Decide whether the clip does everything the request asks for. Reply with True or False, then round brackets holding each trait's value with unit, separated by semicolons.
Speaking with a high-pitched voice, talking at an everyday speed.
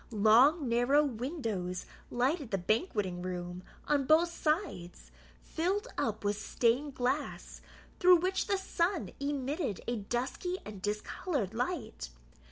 False (255 Hz; 120 wpm)